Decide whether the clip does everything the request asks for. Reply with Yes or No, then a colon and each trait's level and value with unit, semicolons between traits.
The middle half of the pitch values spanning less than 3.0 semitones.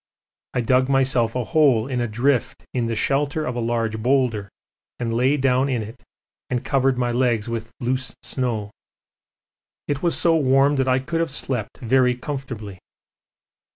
Yes: narrow, 2.6 semitones